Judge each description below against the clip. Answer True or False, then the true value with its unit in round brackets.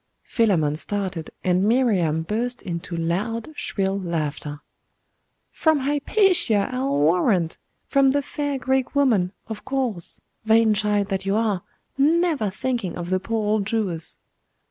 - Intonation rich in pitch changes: True (6.0 semitones)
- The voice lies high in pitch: True (210 Hz)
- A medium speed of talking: False (130 wpm)